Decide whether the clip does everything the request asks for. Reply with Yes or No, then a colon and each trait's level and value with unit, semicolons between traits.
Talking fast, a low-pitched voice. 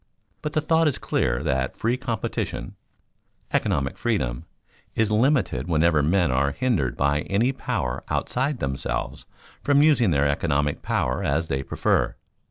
No: average, 140 wpm; very low, 85 Hz